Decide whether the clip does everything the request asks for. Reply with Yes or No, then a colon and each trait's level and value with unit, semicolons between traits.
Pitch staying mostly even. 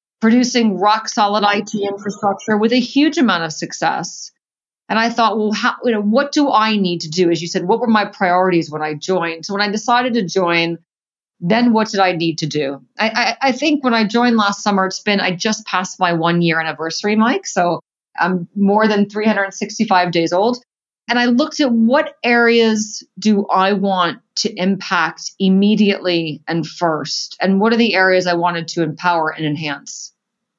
No: average, 4.4 semitones